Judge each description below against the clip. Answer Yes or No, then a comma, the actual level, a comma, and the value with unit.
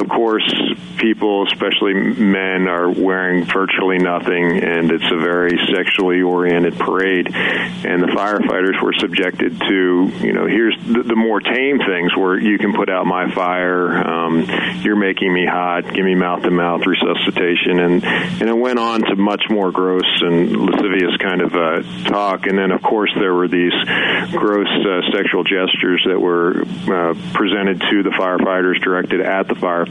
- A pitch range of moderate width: No, narrow, 1.8 semitones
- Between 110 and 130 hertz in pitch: No, very low, 90 Hz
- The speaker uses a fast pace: No, average, 170 wpm